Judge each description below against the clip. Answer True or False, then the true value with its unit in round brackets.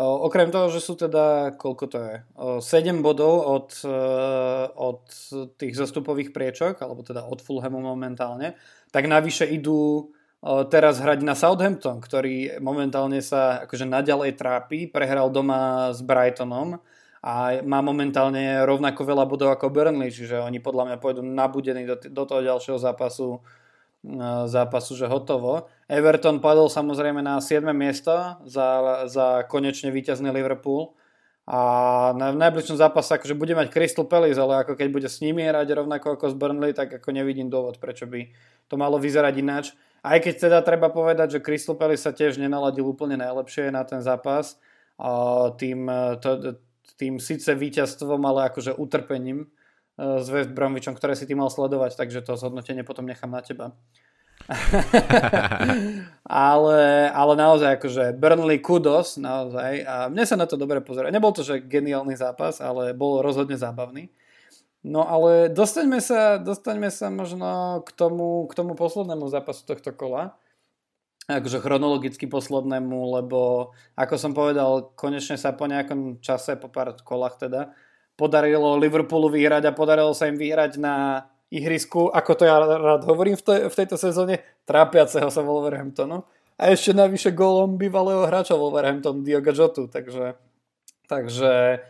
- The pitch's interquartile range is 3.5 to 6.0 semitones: False (3.0 semitones)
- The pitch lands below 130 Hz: False (140 Hz)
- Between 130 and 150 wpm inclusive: True (145 wpm)